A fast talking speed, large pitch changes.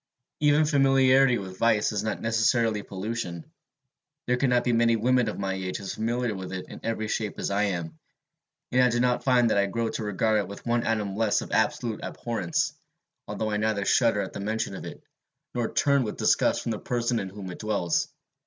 No: fast, 210 wpm; average, 3.1 semitones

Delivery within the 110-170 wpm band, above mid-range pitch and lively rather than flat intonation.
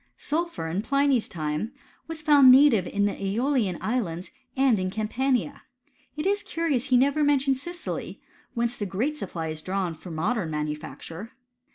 Yes: average, 160 wpm; high, 235 Hz; wide, 7.2 semitones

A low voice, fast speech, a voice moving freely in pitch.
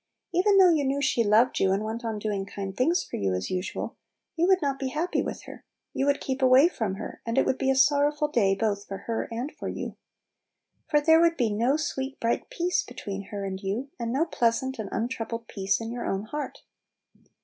No: high, 240 Hz; fast, 225 wpm; wide, 5.7 semitones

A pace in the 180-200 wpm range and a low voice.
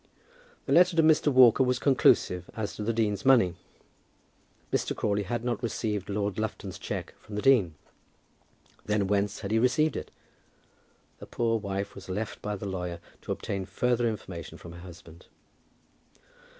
No: average, 160 wpm; low, 105 Hz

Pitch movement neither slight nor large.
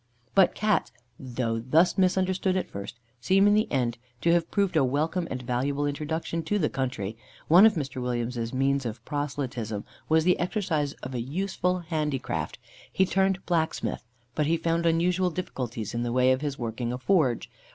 No: wide, 6.2 semitones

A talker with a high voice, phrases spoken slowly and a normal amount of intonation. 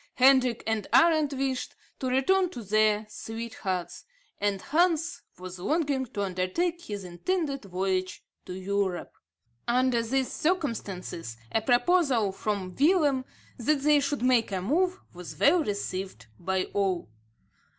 No: high, 235 Hz; slow, 130 wpm; wide, 7.0 semitones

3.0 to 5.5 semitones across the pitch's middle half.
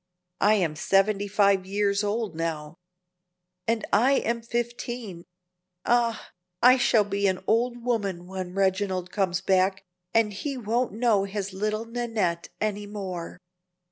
Yes: average, 3.3 semitones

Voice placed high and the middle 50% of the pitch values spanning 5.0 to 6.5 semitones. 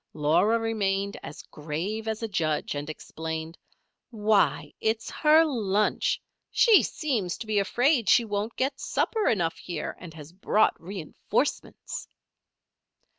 Yes: high, 205 Hz; wide, 5.5 semitones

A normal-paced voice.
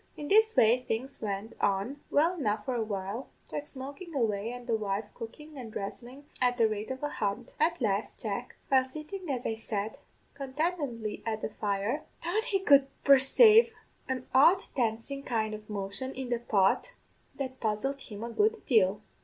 Yes: average, 180 wpm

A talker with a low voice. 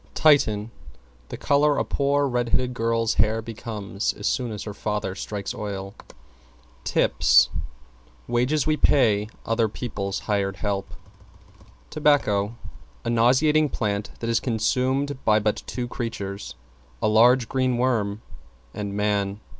Yes: low, 115 Hz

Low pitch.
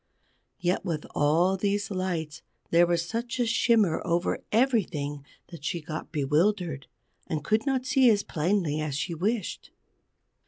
No: medium, 175 Hz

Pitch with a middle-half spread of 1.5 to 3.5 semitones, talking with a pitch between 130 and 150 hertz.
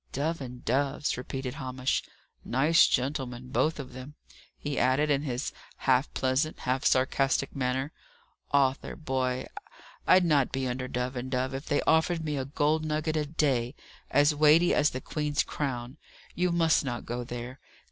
Yes: average, 2.9 semitones; low, 135 Hz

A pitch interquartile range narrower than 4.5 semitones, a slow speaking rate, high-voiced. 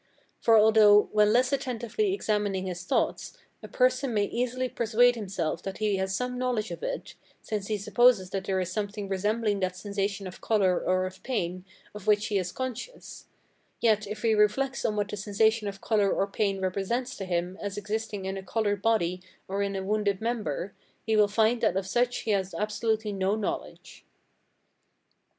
No: average, 2.7 semitones; average, 185 wpm; high, 210 Hz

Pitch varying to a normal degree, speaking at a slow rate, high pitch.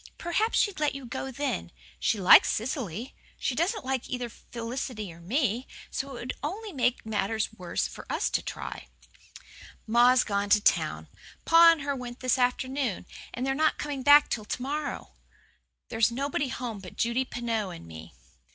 No: average, 4.1 semitones; average, 170 wpm; very high, 250 Hz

